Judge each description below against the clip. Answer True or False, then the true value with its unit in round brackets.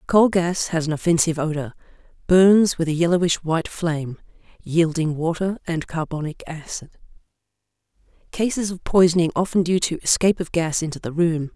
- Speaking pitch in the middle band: True (170 Hz)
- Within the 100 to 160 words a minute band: True (150 wpm)